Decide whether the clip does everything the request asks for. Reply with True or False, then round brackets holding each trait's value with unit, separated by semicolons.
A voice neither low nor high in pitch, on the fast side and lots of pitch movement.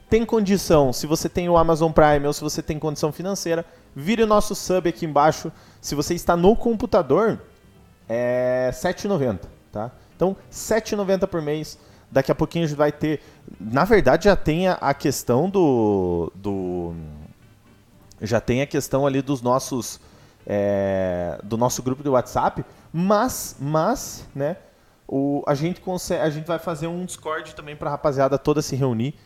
False (150 Hz; 165 wpm; 5.9 semitones)